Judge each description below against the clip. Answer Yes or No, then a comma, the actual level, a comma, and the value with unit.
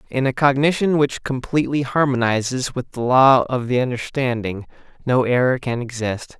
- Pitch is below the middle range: Yes, low, 130 Hz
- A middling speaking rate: Yes, average, 150 wpm